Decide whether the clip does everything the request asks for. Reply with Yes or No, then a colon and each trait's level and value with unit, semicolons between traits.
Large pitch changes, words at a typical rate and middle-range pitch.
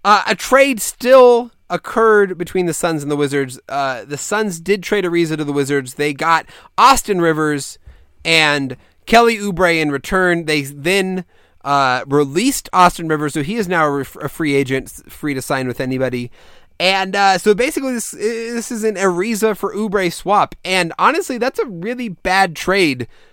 Yes: wide, 6.4 semitones; average, 170 wpm; medium, 180 Hz